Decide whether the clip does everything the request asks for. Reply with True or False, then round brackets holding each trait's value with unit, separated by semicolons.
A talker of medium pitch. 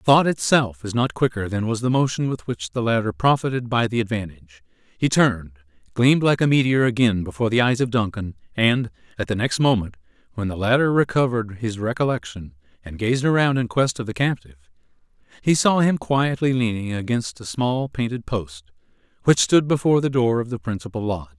False (115 Hz)